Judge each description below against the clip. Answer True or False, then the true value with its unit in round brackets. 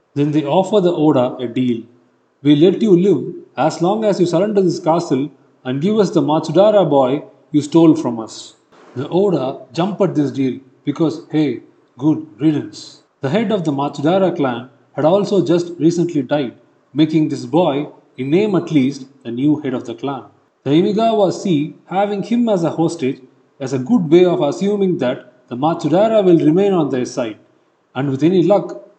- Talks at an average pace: False (180 wpm)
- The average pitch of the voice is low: False (155 Hz)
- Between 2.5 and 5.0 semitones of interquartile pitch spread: True (4.6 semitones)